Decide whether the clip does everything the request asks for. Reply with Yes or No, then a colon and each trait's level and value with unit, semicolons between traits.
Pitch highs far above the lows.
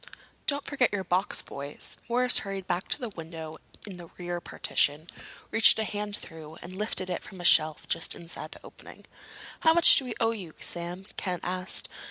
No: average, 4.1 semitones